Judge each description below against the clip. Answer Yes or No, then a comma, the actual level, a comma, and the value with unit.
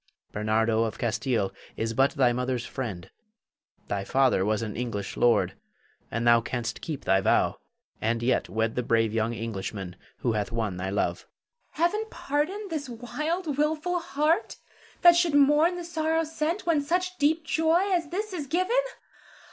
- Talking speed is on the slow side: No, average, 165 wpm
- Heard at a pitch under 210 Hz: Yes, low, 135 Hz